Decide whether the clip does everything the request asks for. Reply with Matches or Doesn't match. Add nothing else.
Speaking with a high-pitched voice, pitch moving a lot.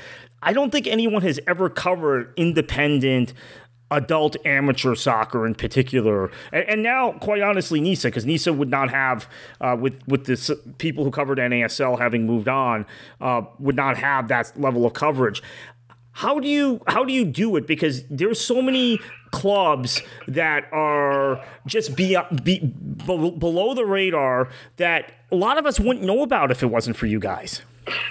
Doesn't match